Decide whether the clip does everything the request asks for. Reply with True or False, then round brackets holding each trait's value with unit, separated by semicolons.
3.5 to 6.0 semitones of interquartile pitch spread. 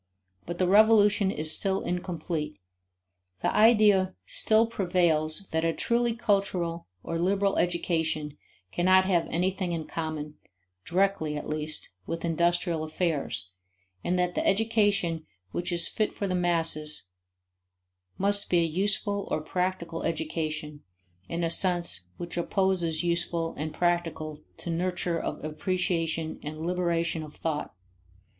False (2.8 semitones)